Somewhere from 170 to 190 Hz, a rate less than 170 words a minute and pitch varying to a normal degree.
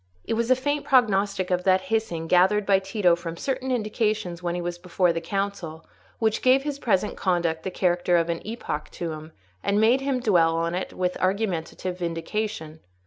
No: medium, 185 Hz; average, 190 wpm; average, 4.2 semitones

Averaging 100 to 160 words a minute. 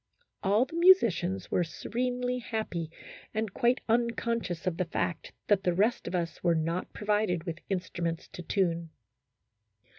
Yes: average, 150 wpm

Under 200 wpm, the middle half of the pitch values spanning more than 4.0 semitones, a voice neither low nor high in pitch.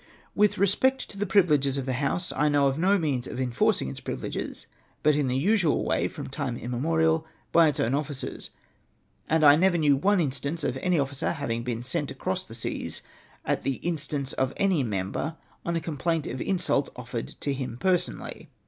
Yes: average, 190 wpm; average, 4.5 semitones; medium, 145 Hz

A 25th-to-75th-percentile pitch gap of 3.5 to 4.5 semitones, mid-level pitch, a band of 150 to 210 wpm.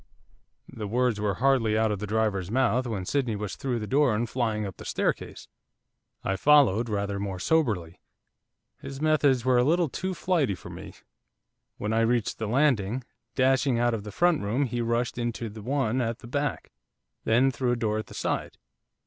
No: average, 3.8 semitones; low, 120 Hz; average, 190 wpm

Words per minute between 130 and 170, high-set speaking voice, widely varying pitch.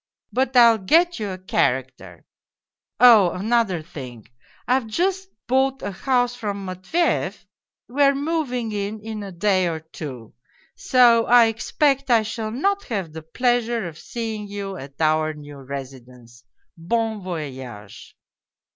Yes: average, 140 wpm; high, 210 Hz; wide, 7.6 semitones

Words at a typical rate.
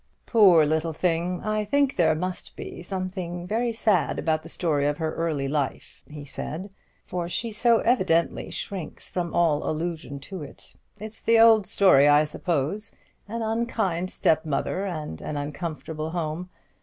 Yes: average, 155 wpm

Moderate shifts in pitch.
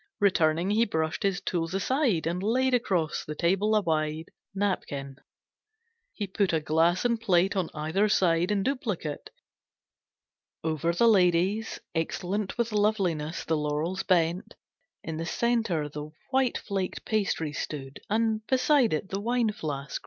Yes: average, 5.0 semitones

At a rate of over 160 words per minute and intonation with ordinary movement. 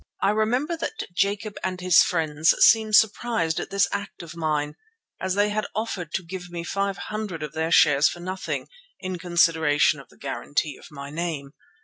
Yes: average, 180 wpm; average, 4.4 semitones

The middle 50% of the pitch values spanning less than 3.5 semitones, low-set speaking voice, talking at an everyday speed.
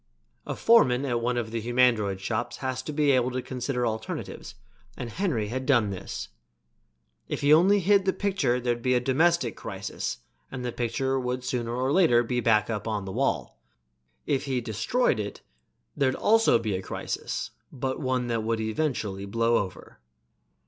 Yes: average, 2.9 semitones; low, 125 Hz; average, 170 wpm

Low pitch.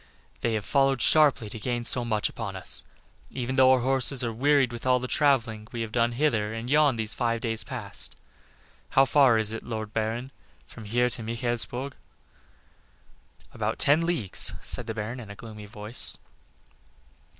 Yes: low, 120 Hz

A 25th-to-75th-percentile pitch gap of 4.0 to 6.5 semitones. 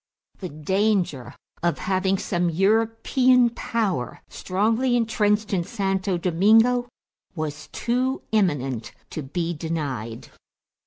Yes: wide, 5.5 semitones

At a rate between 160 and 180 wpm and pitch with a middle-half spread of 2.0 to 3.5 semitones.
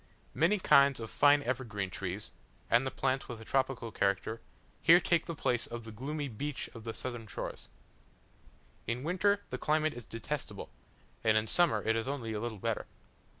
No: average, 175 wpm; average, 4.5 semitones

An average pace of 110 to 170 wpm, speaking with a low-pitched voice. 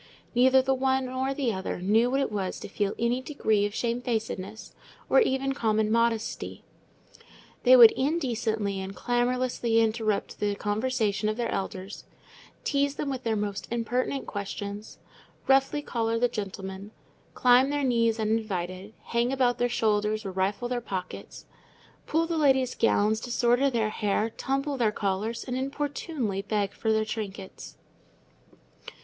No: average, 145 wpm; high, 230 Hz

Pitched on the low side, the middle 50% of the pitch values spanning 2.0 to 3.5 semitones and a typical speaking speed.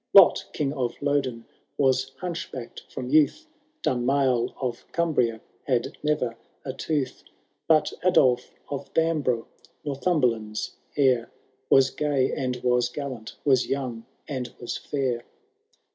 No: low, 130 Hz; average, 2.9 semitones; slow, 115 wpm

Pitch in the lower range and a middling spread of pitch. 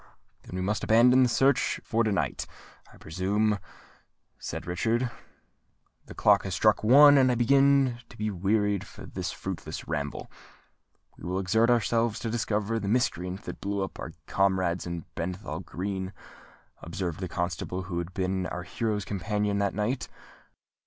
Yes: low, 100 Hz; average, 3.8 semitones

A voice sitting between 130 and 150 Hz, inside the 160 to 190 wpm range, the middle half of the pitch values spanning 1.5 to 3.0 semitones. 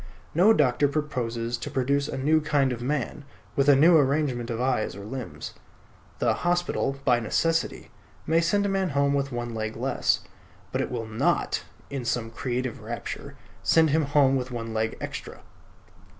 No: low, 135 Hz; average, 170 wpm; average, 3.9 semitones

